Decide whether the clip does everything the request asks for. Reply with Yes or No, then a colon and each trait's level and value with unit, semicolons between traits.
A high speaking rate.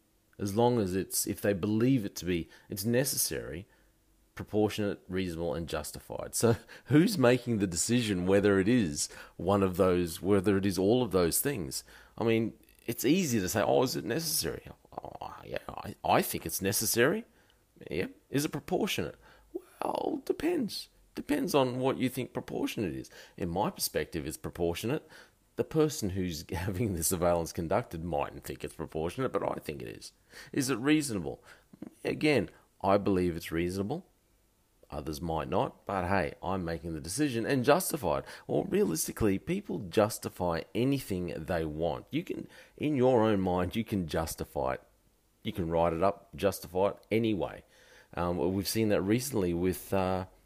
No: average, 165 wpm